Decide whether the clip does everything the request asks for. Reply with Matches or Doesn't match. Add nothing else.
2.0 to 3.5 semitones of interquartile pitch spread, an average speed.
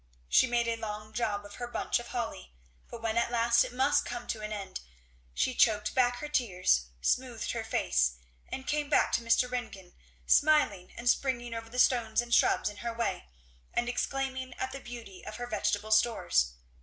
Matches